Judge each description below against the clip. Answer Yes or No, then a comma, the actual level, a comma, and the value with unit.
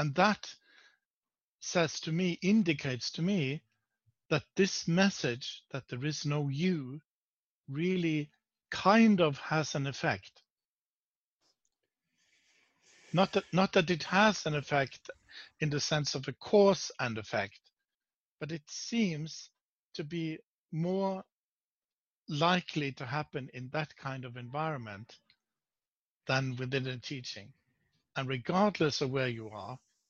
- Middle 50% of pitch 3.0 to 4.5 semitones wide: No, average, 5.2 semitones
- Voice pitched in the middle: Yes, medium, 155 Hz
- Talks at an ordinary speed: No, slow, 125 wpm